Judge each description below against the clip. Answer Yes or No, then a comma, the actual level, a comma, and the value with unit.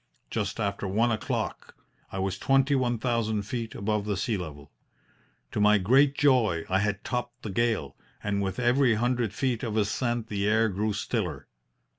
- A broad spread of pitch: No, average, 3.2 semitones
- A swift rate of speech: No, average, 170 wpm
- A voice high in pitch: No, low, 110 Hz